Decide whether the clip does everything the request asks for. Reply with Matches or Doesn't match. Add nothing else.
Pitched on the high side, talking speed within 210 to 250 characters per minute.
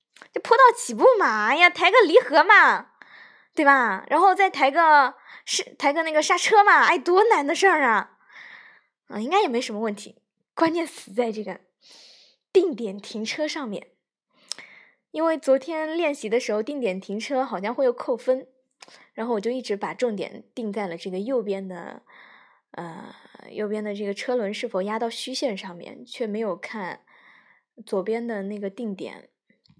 Matches